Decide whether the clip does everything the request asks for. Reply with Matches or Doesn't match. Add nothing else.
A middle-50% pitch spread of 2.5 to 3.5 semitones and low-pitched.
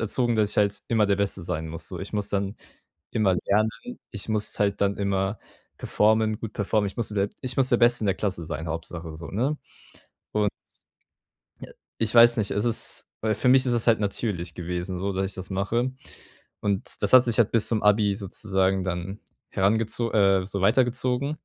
Matches